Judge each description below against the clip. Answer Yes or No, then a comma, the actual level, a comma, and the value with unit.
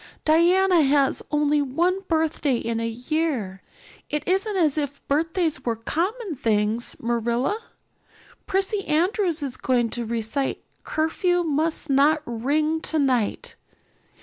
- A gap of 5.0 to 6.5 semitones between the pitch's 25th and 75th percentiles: Yes, wide, 5.4 semitones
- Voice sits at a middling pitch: No, very high, 295 Hz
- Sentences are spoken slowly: Yes, slow, 120 wpm